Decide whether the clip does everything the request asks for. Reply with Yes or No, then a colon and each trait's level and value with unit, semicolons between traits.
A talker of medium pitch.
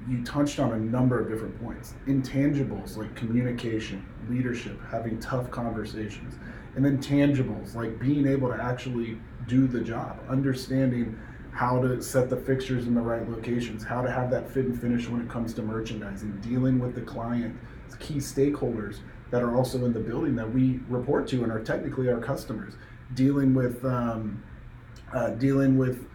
No: low, 120 Hz